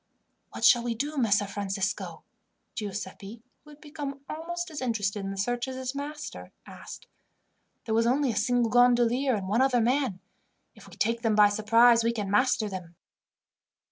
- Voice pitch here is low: No, high, 235 Hz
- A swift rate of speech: No, average, 175 wpm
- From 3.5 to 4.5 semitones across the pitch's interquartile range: Yes, average, 4.0 semitones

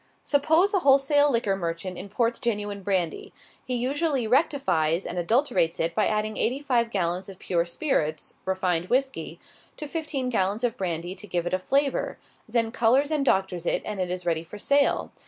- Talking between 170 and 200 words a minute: Yes, average, 175 wpm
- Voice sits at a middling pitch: No, high, 215 Hz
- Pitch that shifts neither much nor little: No, wide, 7.0 semitones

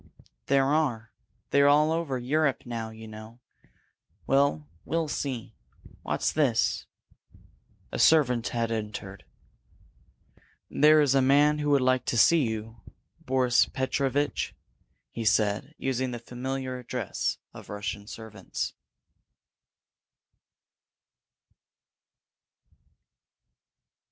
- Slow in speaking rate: Yes, slow, 90 wpm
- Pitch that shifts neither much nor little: Yes, average, 4.1 semitones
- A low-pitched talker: Yes, low, 130 Hz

